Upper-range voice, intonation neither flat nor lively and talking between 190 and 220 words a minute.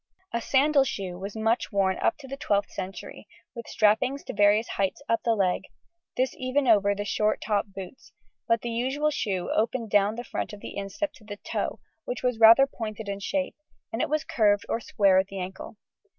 Yes: high, 220 Hz; average, 4.1 semitones; fast, 205 wpm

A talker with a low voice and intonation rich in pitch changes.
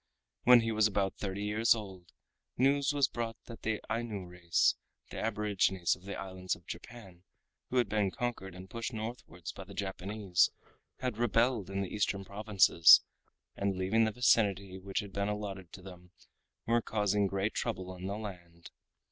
No: low, 100 Hz; average, 3.1 semitones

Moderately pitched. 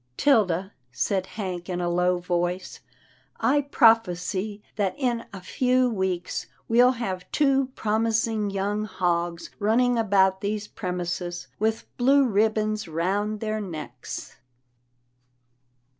No: high, 205 Hz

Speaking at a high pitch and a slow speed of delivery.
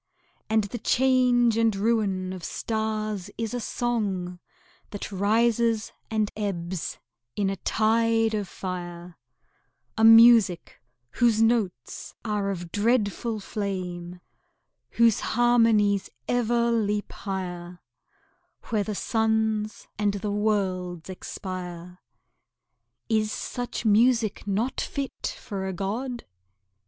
Yes: high, 210 Hz; slow, 105 wpm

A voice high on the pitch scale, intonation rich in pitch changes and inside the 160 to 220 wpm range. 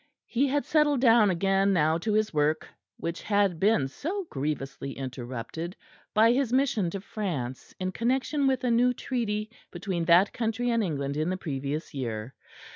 Yes: high, 195 Hz; wide, 7.6 semitones; average, 165 wpm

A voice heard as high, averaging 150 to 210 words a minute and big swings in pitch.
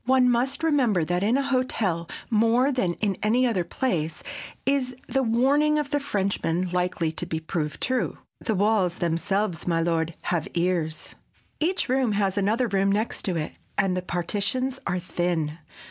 Yes: high, 200 Hz; average, 160 wpm; wide, 6.6 semitones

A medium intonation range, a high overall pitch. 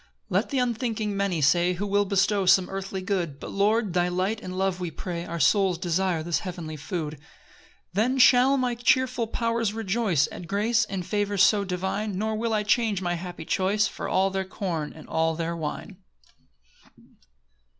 Yes: average, 3.5 semitones; high, 195 Hz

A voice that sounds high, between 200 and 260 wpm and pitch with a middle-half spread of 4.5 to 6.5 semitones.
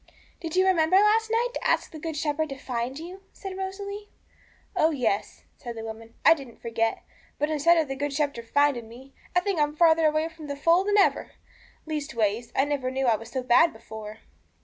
Yes: very high, 295 Hz; fast, 205 wpm; wide, 5.6 semitones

